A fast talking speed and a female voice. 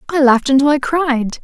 Yes: fast, 210 wpm; female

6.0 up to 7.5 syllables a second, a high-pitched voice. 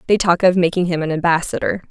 No: 6.6 syllables/s; medium, 175 Hz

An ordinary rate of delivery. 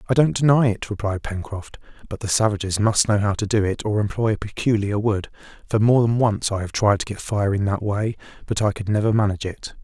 No: fast, 240 wpm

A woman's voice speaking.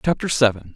No: male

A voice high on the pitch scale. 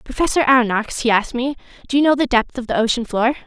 Yes: very high, 250 Hz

